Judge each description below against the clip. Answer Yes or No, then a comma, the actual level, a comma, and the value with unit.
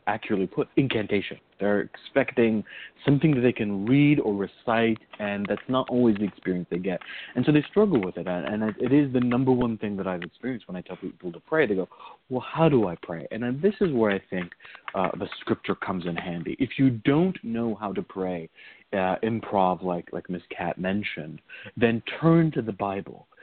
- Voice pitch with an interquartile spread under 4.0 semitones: No, average, 5.1 semitones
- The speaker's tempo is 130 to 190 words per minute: No, fast, 205 wpm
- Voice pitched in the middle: No, low, 110 Hz